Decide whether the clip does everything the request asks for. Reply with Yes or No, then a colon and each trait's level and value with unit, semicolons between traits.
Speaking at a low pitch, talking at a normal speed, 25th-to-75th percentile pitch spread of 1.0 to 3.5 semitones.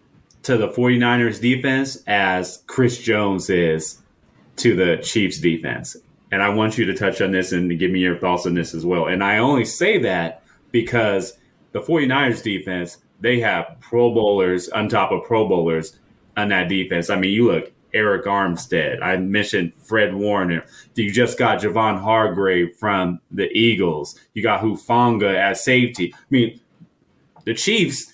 No: low, 100 Hz; average, 165 wpm; average, 4.3 semitones